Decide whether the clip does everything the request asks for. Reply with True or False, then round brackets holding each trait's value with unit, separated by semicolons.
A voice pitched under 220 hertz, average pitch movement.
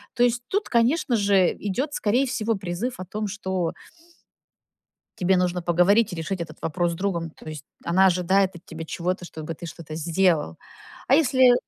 True (185 Hz; 4.8 semitones)